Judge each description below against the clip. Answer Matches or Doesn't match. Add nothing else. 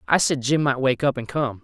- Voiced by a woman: Doesn't match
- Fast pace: Matches